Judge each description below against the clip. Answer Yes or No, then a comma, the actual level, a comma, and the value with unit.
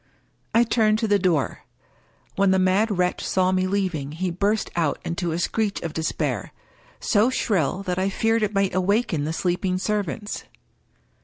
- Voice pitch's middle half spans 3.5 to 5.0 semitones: No, average, 3.0 semitones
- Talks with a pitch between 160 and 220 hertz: Yes, high, 190 Hz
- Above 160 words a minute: Yes, average, 175 wpm